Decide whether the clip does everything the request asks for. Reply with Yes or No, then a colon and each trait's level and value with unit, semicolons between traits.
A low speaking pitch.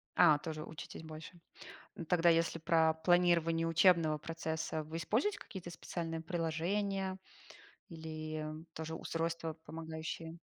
No: medium, 165 Hz